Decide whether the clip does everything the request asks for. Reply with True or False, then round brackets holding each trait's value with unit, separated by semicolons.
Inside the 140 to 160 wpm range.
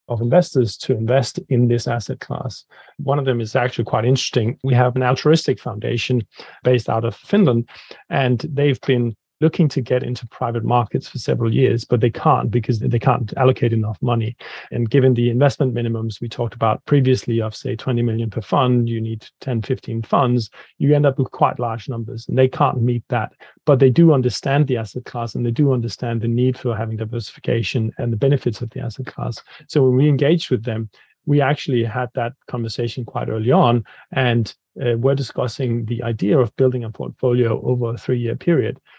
False (200 wpm)